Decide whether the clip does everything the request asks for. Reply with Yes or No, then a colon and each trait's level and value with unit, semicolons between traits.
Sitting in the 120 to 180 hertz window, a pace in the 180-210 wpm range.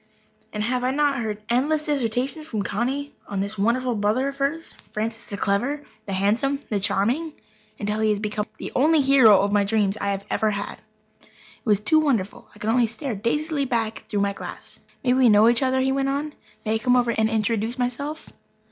No: high, 235 Hz; average, 200 wpm